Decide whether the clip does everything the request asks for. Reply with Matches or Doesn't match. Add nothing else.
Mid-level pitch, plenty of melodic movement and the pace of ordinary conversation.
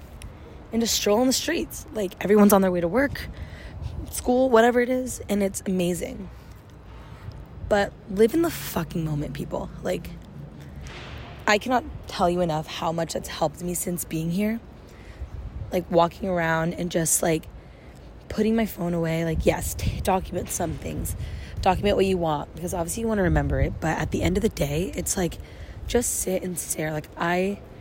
Doesn't match